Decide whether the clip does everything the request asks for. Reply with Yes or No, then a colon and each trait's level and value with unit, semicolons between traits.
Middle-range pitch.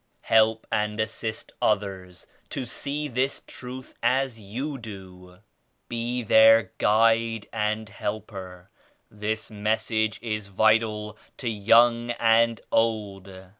No: low, 110 Hz